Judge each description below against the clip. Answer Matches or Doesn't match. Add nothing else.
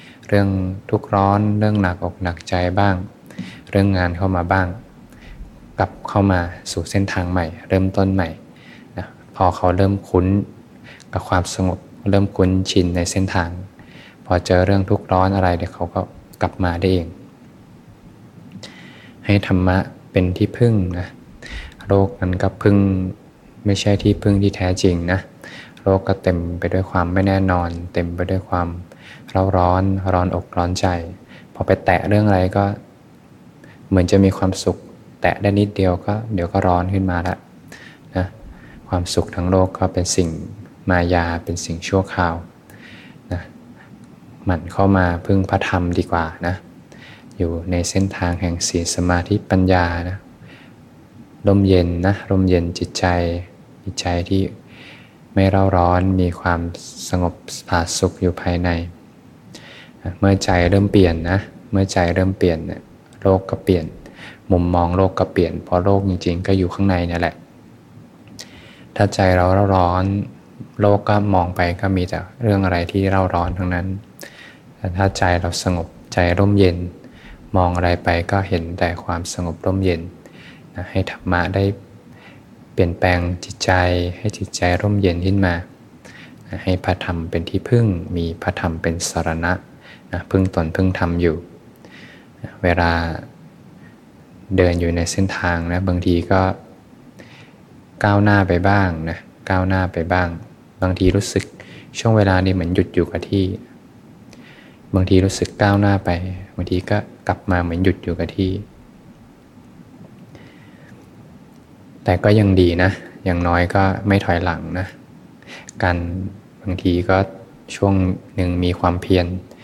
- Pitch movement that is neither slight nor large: Doesn't match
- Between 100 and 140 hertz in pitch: Doesn't match